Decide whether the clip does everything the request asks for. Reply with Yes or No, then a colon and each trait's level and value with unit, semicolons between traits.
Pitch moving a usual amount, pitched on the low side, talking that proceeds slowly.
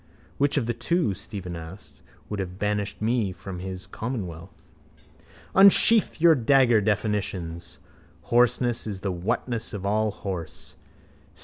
Yes: average, 4.2 semitones; low, 105 Hz; slow, 120 wpm